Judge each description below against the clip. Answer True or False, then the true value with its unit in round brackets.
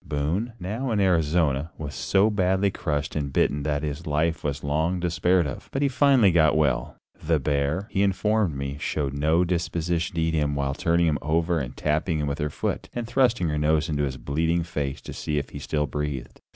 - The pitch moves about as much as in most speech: True (3.6 semitones)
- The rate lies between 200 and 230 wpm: True (205 wpm)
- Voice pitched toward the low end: True (80 Hz)